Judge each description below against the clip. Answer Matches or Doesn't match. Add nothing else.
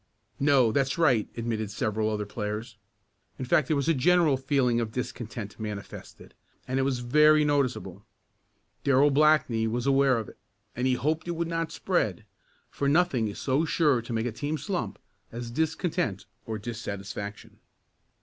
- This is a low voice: Matches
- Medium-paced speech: Matches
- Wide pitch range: Doesn't match